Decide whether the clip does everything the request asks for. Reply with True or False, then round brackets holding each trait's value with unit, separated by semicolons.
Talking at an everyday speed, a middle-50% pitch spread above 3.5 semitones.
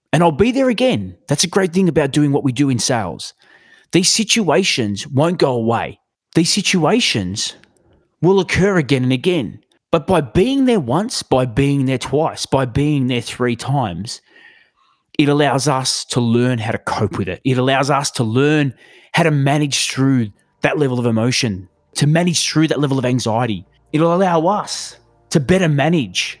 True (175 wpm; 5.1 semitones)